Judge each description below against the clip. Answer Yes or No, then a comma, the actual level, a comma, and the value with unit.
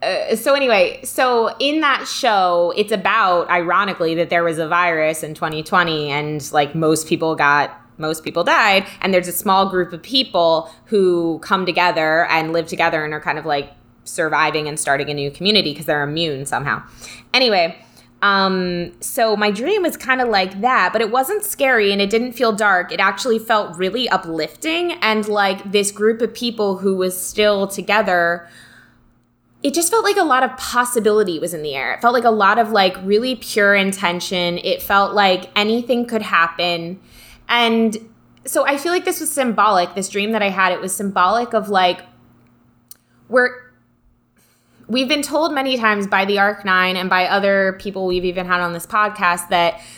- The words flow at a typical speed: Yes, average, 185 wpm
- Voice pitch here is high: Yes, high, 195 Hz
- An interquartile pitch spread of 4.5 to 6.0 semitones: Yes, average, 4.9 semitones